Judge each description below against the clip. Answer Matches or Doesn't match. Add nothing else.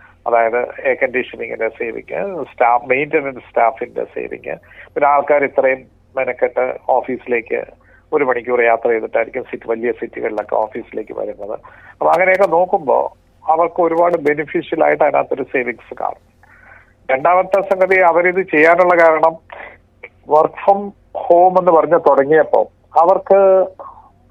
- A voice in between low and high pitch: Matches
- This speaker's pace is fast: Doesn't match